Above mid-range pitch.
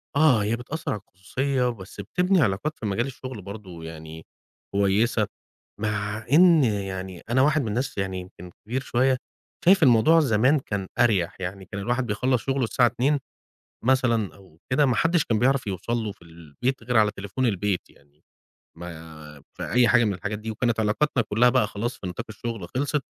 No: low, 110 Hz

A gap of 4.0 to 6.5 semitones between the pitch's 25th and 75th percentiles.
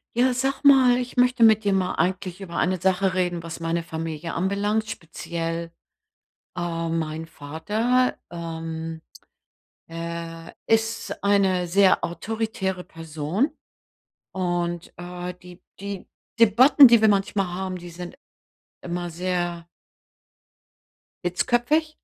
Yes: average, 4.4 semitones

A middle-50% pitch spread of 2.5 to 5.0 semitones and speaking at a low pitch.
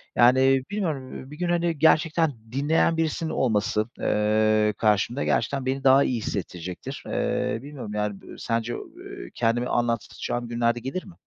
No: wide, 5.6 semitones; low, 130 Hz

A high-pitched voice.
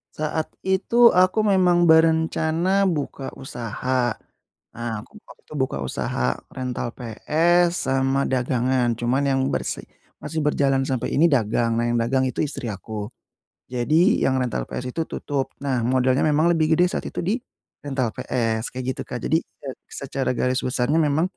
No: low, 135 Hz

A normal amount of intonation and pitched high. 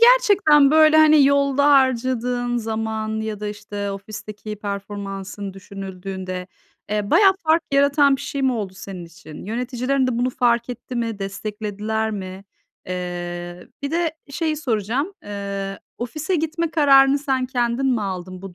No: wide, 5.8 semitones; high, 225 Hz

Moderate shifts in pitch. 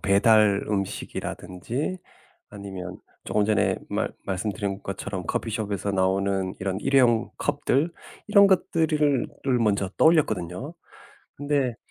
No: wide, 6.3 semitones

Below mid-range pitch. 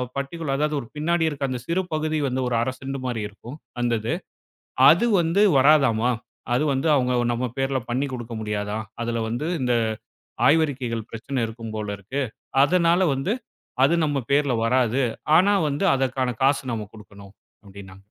Yes: low, 130 Hz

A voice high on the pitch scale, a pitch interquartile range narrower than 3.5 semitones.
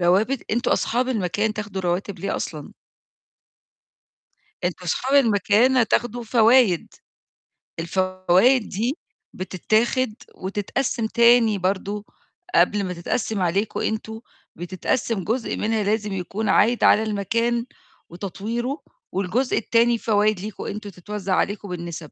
No: high, 210 Hz; average, 3.8 semitones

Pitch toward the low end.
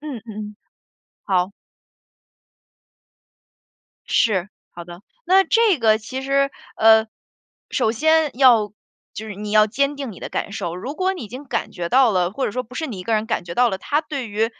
No: high, 225 Hz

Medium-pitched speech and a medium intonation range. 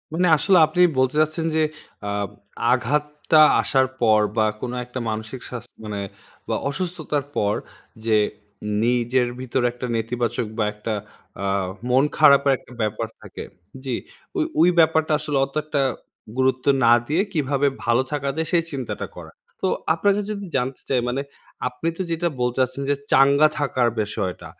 No: low, 130 Hz; average, 4.1 semitones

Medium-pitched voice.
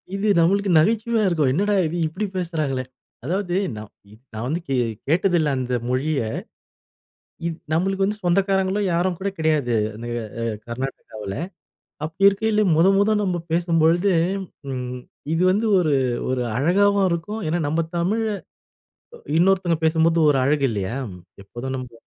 Yes: medium, 170 Hz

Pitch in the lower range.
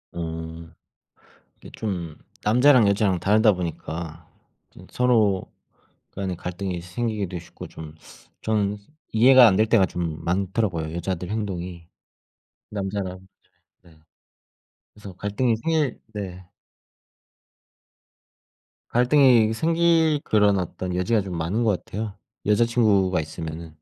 Yes: low, 100 Hz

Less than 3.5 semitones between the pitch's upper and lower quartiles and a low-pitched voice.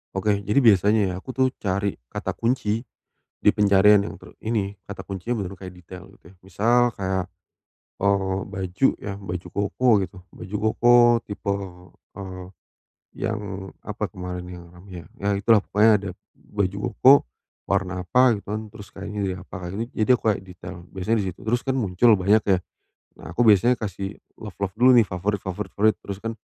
Yes: narrow, 2.6 semitones; low, 100 Hz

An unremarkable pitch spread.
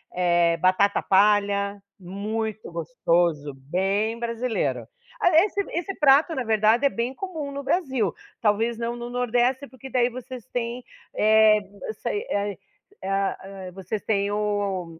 Yes: average, 4.2 semitones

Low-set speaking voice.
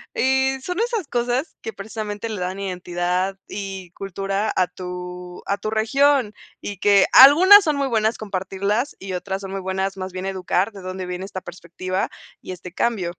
No: high, 195 Hz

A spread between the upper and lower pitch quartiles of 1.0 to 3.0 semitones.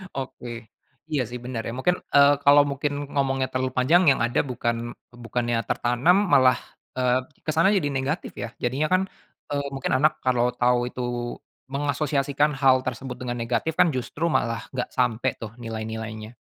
Yes: average, 2.7 semitones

